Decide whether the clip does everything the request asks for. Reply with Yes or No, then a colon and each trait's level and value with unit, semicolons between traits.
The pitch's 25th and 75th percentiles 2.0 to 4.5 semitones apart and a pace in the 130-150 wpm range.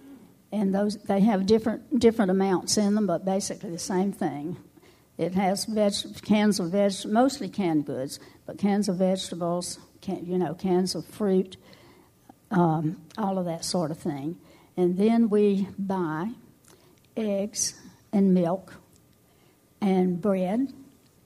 Yes: average, 2.9 semitones; average, 140 wpm